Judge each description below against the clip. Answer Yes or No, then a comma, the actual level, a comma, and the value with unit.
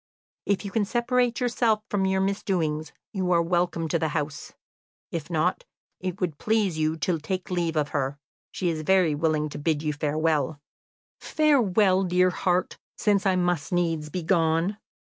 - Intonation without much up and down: No, average, 3.7 semitones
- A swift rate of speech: No, average, 170 wpm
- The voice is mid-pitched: Yes, medium, 175 Hz